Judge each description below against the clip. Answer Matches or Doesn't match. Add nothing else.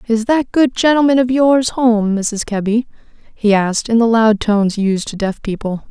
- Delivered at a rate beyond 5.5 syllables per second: Doesn't match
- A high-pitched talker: Matches